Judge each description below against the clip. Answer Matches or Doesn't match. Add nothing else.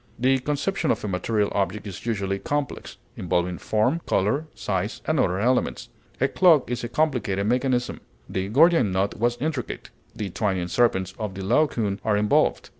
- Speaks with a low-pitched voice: Matches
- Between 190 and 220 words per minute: Doesn't match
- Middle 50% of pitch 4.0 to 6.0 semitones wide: Matches